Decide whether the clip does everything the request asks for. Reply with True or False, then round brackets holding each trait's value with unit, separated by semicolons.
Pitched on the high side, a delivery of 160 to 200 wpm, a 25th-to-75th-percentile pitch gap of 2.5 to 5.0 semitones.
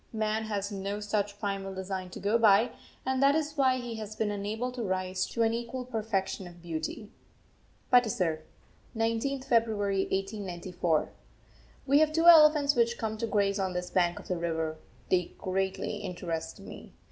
True (205 Hz; 165 wpm; 3.8 semitones)